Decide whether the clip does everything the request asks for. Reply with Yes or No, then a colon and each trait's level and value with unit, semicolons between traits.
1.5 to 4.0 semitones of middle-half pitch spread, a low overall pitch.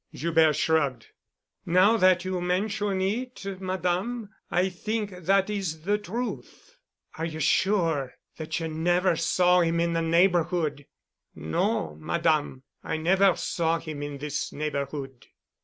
No: average, 3.4 semitones; medium, 170 Hz